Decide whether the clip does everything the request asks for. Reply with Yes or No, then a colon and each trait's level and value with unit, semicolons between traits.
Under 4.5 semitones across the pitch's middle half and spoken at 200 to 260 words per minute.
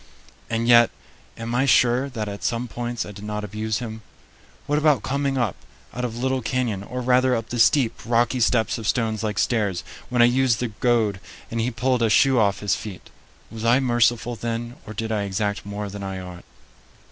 Yes: average, 2.7 semitones; fast, 205 wpm